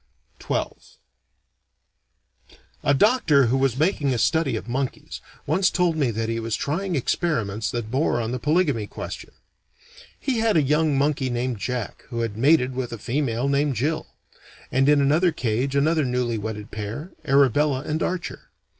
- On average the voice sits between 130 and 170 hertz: Yes, low, 135 Hz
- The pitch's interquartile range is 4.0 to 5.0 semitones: Yes, average, 4.6 semitones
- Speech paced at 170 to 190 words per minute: No, average, 160 wpm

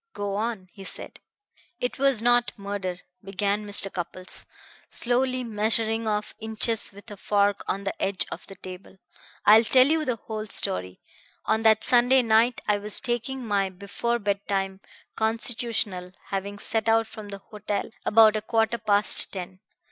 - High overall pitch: Yes, high, 210 Hz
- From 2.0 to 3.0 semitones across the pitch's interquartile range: Yes, narrow, 2.5 semitones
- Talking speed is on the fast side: No, average, 160 wpm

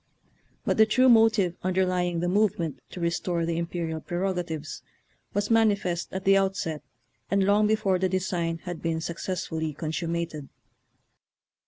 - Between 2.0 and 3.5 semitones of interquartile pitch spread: Yes, average, 2.8 semitones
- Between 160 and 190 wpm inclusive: No, average, 145 wpm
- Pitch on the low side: No, medium, 180 Hz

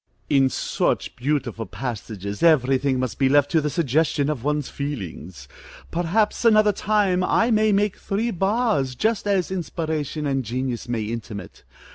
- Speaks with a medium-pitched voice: Yes, medium, 145 Hz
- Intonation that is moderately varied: No, wide, 7.1 semitones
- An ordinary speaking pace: Yes, average, 150 wpm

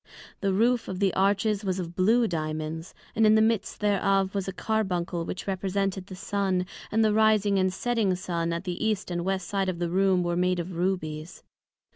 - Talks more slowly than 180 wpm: No, average, 200 wpm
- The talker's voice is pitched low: No, high, 190 Hz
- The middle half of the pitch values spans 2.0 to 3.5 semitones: Yes, narrow, 2.4 semitones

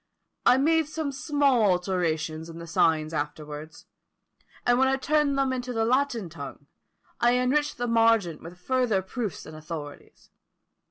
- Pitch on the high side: Yes, high, 225 Hz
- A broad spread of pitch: Yes, wide, 8.3 semitones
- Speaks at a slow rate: No, average, 150 wpm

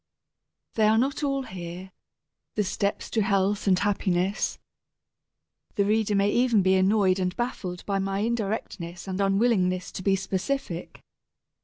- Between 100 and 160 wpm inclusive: Yes, average, 140 wpm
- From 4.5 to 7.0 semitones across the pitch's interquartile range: No, narrow, 2.6 semitones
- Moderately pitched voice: No, high, 195 Hz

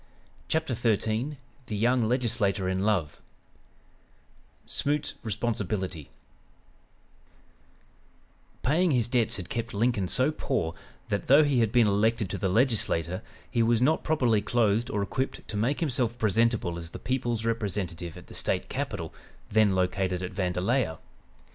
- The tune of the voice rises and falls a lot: No, average, 4.3 semitones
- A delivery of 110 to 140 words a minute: Yes, slow, 135 wpm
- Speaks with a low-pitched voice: Yes, low, 110 Hz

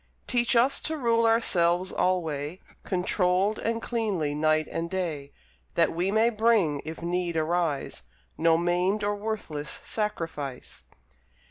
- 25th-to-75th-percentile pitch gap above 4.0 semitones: Yes, average, 5.2 semitones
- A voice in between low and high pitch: Yes, medium, 180 Hz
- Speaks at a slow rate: Yes, slow, 125 wpm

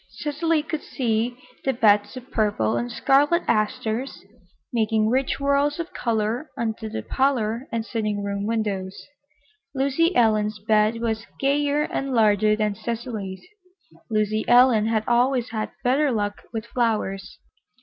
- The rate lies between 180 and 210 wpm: No, slow, 135 wpm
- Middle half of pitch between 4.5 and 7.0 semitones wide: No, average, 3.8 semitones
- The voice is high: Yes, high, 230 Hz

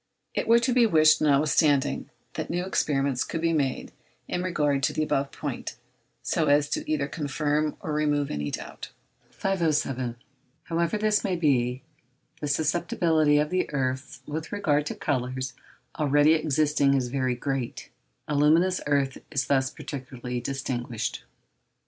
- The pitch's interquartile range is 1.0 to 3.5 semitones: Yes, average, 2.9 semitones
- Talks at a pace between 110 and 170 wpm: Yes, average, 145 wpm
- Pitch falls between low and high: Yes, medium, 145 Hz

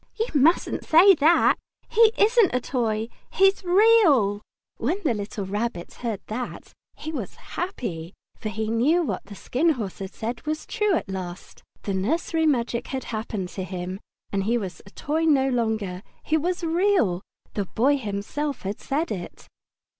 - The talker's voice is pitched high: Yes, high, 240 Hz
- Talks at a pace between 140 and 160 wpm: No, average, 170 wpm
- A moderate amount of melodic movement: No, wide, 8.0 semitones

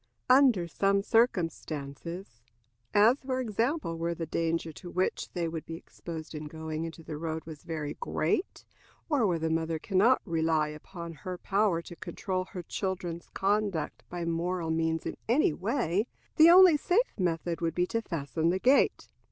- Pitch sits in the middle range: Yes, medium, 170 Hz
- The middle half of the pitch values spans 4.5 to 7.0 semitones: No, average, 4.0 semitones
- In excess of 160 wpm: Yes, average, 170 wpm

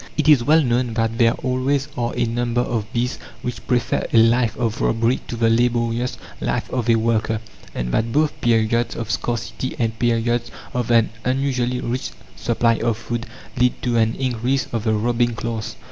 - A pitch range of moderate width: No, narrow, 1.5 semitones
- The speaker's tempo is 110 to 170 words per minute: No, average, 180 wpm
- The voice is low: Yes, low, 120 Hz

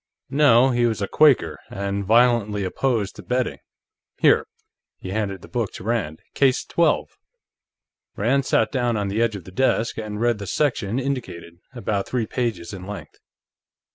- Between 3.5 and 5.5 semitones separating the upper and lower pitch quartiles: Yes, average, 3.9 semitones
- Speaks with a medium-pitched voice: No, low, 115 Hz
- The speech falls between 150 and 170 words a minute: Yes, average, 165 wpm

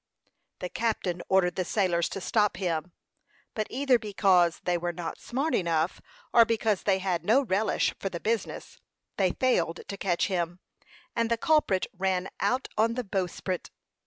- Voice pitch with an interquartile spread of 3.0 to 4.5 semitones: Yes, average, 4.1 semitones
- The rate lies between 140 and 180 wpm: Yes, average, 160 wpm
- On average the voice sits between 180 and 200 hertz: Yes, high, 190 Hz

